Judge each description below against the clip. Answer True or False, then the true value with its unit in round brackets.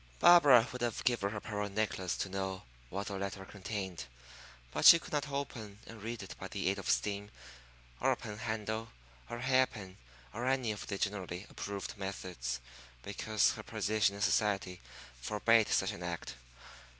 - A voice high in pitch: False (105 Hz)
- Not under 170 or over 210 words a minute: True (175 wpm)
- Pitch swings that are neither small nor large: True (3.0 semitones)